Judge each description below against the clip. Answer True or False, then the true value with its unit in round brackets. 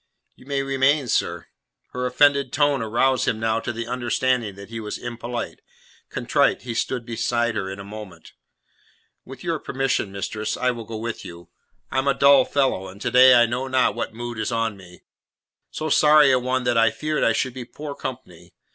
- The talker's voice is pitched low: True (120 Hz)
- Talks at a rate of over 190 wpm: True (200 wpm)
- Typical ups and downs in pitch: True (3.0 semitones)